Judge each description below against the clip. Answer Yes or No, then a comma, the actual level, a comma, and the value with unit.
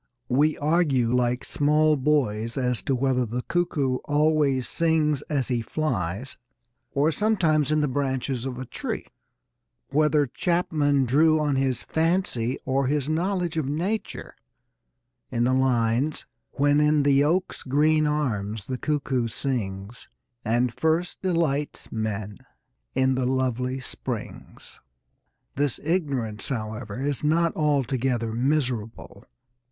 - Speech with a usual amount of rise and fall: Yes, average, 3.6 semitones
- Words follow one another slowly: Yes, slow, 125 wpm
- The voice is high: No, low, 135 Hz